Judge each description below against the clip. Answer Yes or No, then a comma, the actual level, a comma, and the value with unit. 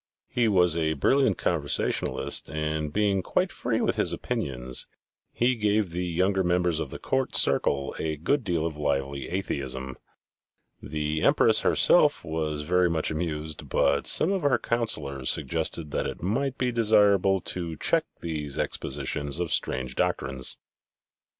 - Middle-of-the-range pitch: No, very low, 80 Hz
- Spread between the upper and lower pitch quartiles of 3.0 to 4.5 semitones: No, average, 5.2 semitones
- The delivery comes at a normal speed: Yes, average, 145 wpm